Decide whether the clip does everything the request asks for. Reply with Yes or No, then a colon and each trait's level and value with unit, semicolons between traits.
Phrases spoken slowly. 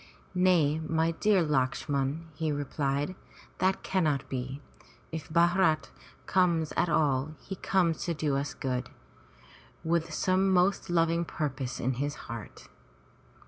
Yes: slow, 125 wpm